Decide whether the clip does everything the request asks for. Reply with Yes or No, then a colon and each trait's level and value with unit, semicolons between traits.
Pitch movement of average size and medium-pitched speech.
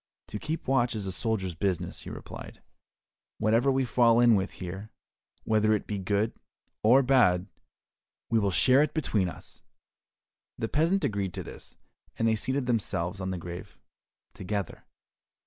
No: average, 4.6 semitones; low, 110 Hz